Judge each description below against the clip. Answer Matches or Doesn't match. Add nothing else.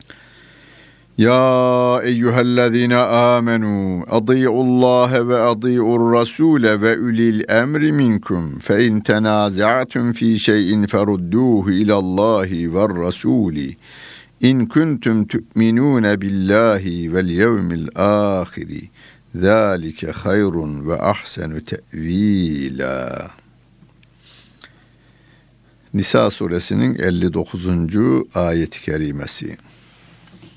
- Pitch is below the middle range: Matches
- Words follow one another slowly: Matches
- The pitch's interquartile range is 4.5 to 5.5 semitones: Matches